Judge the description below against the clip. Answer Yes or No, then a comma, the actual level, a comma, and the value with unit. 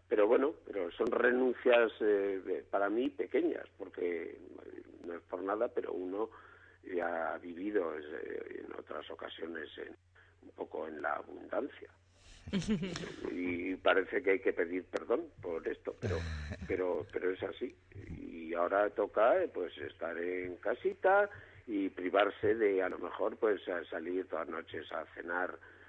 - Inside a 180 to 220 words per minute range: No, average, 155 wpm